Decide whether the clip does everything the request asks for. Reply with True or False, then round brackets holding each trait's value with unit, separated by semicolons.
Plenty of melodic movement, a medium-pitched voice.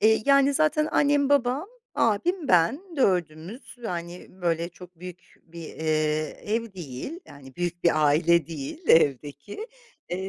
True (8.1 semitones; 180 Hz)